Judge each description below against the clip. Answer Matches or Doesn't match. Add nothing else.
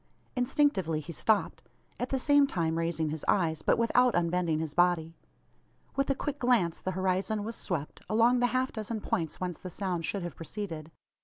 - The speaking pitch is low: Doesn't match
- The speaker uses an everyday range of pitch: Doesn't match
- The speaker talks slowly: Doesn't match